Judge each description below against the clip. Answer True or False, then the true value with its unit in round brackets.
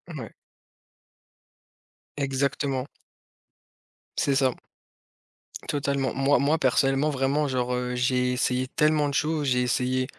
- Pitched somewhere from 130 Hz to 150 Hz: True (135 Hz)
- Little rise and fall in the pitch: True (2.0 semitones)